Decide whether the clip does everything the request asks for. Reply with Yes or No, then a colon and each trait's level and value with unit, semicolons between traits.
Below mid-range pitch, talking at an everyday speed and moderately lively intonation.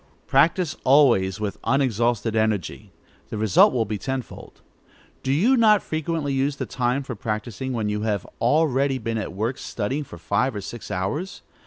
Yes: low, 120 Hz; average, 165 wpm; average, 4.6 semitones